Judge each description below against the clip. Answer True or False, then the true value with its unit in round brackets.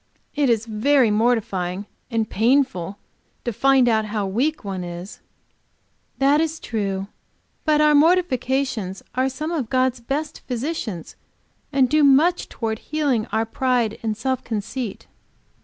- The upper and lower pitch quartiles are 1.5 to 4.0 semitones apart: False (4.6 semitones)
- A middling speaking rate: False (130 wpm)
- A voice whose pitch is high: True (245 Hz)